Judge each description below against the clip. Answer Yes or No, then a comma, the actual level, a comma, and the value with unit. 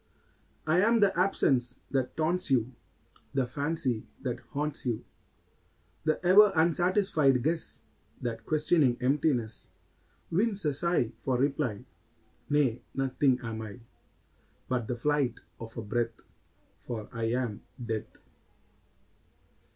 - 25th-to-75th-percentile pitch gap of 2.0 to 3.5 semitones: No, average, 4.8 semitones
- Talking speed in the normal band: No, slow, 115 wpm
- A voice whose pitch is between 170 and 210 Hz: No, low, 135 Hz